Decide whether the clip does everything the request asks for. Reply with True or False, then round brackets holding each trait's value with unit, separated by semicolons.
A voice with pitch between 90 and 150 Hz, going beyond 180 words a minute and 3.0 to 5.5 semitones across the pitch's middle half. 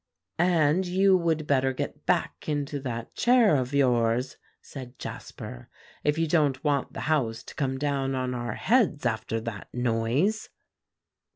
False (140 Hz; 150 wpm; 4.3 semitones)